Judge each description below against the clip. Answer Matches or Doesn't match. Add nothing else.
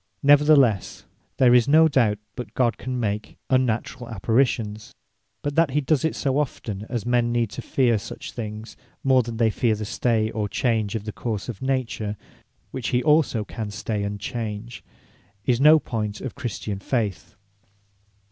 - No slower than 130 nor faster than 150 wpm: Doesn't match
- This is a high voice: Doesn't match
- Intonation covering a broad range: Doesn't match